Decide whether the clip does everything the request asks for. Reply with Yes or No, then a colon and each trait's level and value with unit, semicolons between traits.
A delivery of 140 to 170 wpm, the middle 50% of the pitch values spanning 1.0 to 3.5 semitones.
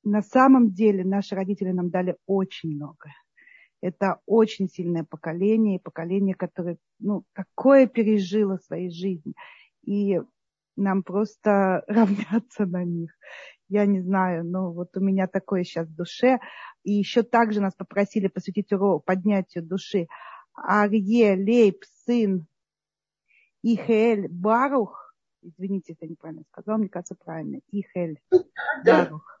No: average, 130 wpm; average, 3.0 semitones